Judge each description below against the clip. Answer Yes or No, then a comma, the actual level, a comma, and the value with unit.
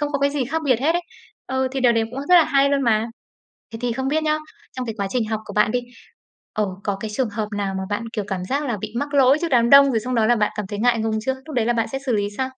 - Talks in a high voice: Yes, high, 245 Hz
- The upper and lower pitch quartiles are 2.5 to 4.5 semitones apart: Yes, average, 4.1 semitones